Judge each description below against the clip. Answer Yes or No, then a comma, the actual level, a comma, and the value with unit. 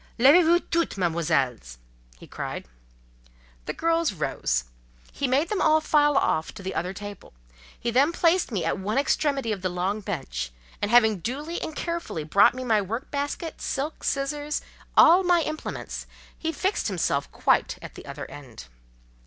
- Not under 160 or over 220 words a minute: Yes, average, 165 wpm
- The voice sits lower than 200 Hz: No, high, 235 Hz